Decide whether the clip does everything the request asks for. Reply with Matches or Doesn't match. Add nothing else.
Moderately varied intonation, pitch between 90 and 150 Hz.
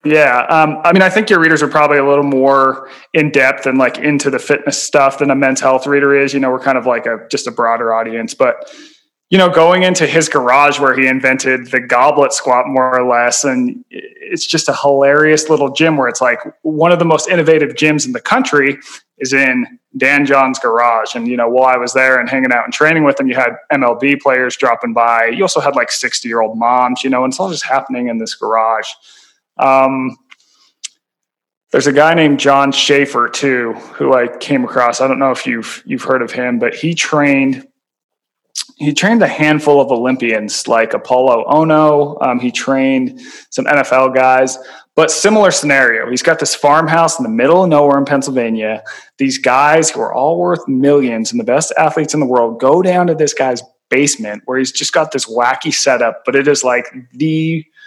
Matches